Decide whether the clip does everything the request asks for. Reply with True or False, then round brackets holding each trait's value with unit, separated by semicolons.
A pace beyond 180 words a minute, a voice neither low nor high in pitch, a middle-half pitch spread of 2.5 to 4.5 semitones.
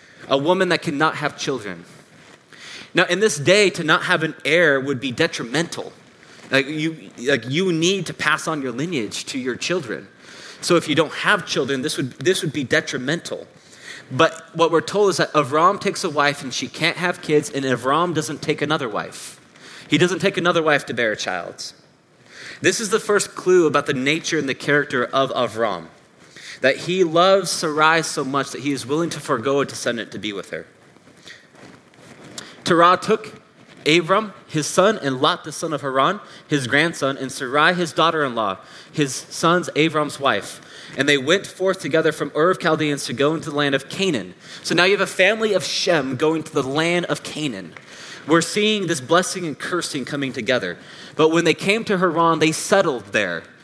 True (195 wpm; 160 Hz; 3.6 semitones)